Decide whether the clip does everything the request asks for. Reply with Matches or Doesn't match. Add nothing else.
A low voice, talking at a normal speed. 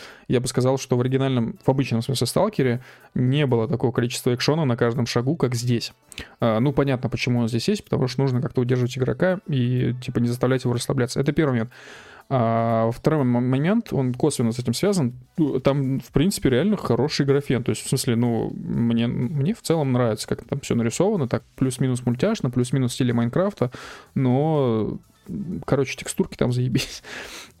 Doesn't match